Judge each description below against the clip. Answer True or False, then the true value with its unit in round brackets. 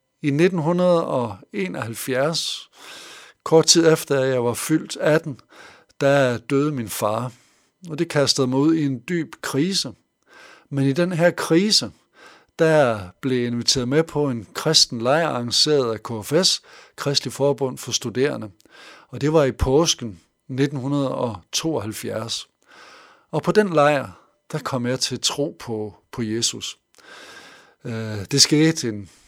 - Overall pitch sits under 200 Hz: True (135 Hz)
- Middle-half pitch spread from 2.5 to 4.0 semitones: False (4.8 semitones)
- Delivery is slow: True (130 wpm)